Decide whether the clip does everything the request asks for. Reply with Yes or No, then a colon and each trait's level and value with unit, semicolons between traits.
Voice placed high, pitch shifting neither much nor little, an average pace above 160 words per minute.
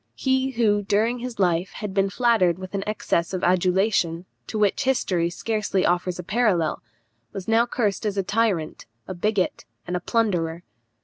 Yes: high, 195 Hz; average, 3.9 semitones; average, 170 wpm